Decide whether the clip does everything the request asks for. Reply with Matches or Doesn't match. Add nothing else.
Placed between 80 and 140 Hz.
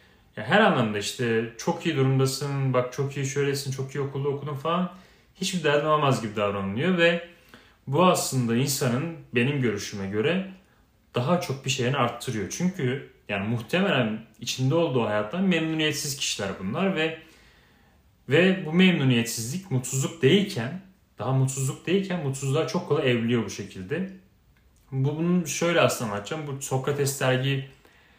Matches